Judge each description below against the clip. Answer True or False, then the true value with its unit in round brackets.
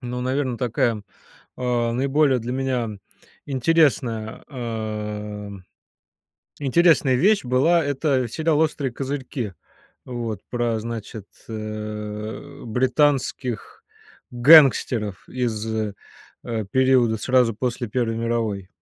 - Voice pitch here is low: True (120 Hz)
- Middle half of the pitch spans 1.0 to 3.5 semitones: True (3.2 semitones)